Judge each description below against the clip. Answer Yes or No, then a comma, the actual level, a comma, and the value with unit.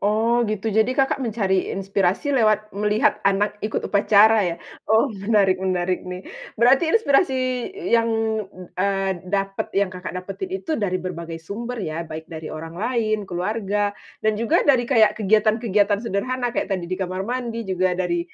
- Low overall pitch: No, high, 205 Hz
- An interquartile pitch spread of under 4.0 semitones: Yes, average, 3.6 semitones